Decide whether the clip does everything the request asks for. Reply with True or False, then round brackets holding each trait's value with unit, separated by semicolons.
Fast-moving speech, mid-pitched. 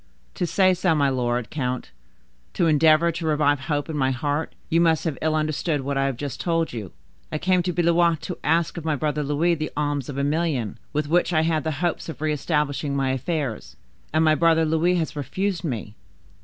True (210 wpm; 155 Hz)